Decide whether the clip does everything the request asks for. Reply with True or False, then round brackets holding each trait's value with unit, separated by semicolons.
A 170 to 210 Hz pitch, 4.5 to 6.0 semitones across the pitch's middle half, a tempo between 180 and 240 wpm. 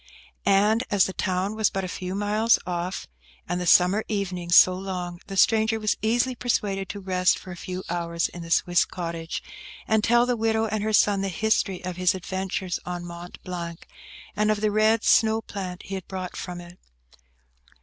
False (190 Hz; 3.1 semitones; 190 wpm)